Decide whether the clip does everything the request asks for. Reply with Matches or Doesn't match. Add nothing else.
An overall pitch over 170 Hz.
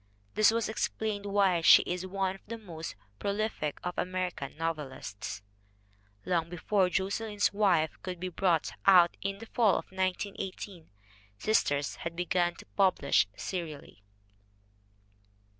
Matches